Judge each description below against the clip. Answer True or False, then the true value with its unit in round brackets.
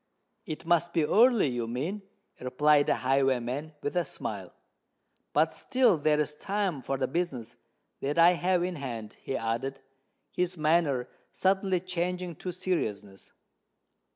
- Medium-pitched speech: True (150 Hz)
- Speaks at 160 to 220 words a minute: False (140 wpm)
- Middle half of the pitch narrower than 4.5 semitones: False (5.5 semitones)